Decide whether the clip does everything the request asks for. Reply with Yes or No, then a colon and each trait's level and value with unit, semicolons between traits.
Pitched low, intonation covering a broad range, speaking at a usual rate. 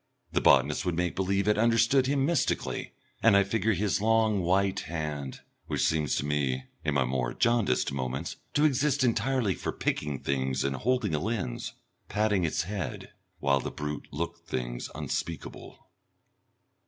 Yes: very low, 90 Hz; wide, 7.5 semitones; average, 155 wpm